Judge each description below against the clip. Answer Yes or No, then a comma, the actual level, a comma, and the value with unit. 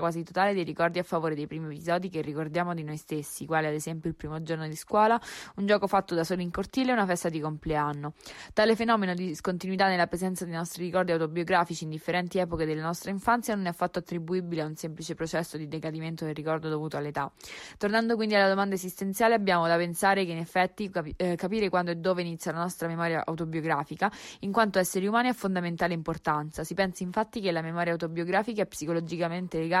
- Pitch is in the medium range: Yes, medium, 175 Hz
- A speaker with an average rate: No, fast, 205 wpm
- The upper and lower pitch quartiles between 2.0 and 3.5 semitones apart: Yes, average, 2.8 semitones